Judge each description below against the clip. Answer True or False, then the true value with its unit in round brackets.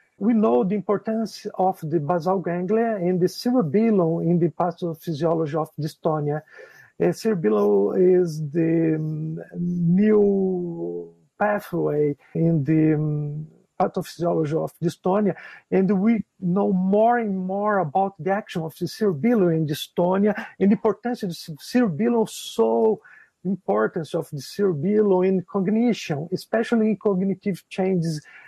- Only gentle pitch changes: False (3.9 semitones)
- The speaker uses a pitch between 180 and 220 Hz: True (185 Hz)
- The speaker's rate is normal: False (120 wpm)